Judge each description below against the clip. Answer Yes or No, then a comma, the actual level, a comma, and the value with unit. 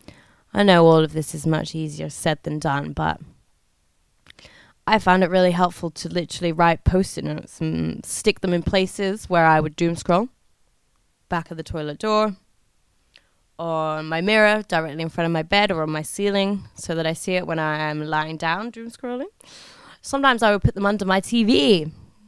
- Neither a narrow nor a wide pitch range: Yes, average, 4.2 semitones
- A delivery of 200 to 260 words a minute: No, average, 190 wpm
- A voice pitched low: No, medium, 165 Hz